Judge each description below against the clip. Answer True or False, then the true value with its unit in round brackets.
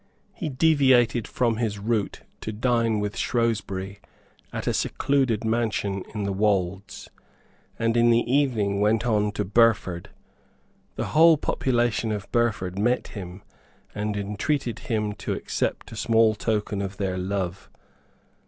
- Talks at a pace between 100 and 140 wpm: True (135 wpm)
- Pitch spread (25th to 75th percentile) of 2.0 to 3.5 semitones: True (2.9 semitones)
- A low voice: True (110 Hz)